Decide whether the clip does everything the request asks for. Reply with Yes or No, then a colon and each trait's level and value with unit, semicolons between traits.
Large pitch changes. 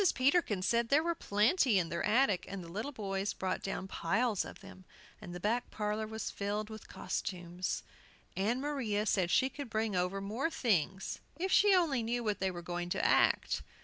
No: average, 4.5 semitones